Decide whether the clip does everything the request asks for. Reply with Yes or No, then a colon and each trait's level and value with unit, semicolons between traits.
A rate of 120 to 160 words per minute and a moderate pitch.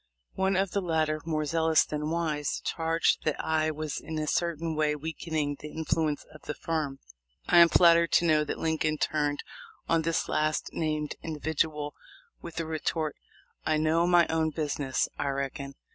No: average, 170 wpm; medium, 155 Hz